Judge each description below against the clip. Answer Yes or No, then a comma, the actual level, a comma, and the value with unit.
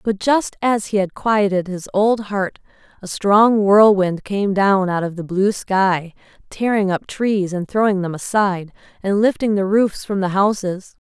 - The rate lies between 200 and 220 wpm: No, average, 180 wpm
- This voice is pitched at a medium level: No, high, 200 Hz